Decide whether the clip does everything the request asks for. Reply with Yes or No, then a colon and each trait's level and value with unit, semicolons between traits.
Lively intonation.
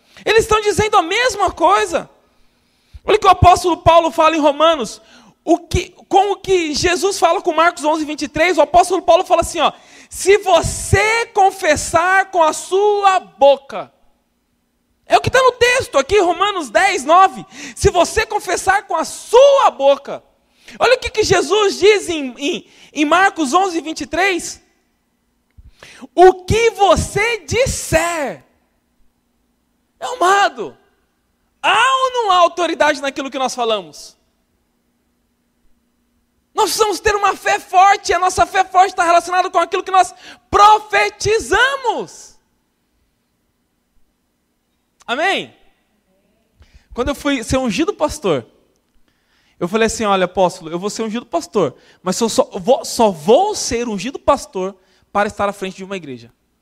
Yes: wide, 6.8 semitones